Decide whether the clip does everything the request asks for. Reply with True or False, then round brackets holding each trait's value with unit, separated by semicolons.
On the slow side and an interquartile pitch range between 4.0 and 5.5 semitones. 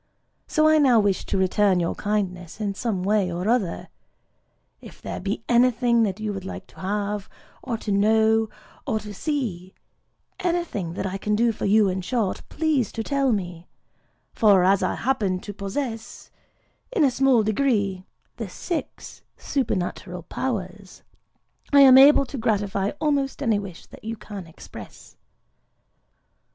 False (150 wpm; 4.5 semitones)